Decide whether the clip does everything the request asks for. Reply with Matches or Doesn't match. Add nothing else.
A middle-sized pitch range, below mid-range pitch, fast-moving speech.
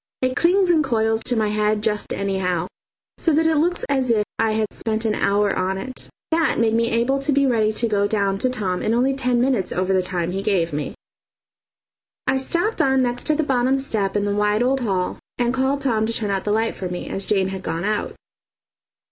Doesn't match